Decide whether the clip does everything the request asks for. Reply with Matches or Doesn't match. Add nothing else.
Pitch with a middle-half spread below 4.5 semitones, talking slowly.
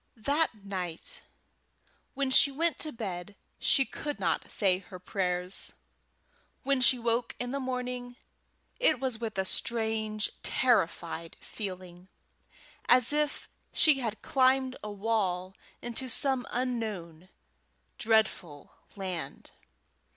Doesn't match